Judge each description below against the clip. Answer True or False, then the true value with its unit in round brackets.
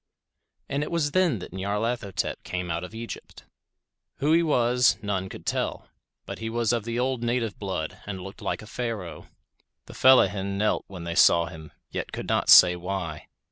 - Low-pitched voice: True (105 Hz)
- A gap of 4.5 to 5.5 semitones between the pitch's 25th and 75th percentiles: True (4.8 semitones)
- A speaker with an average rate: True (180 wpm)